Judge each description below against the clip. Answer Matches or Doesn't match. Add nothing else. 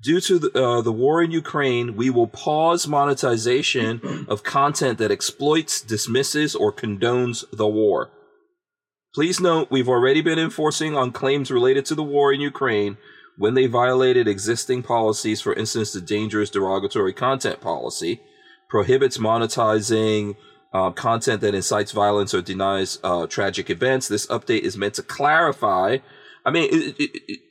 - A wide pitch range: Matches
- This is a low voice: Matches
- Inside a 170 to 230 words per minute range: Doesn't match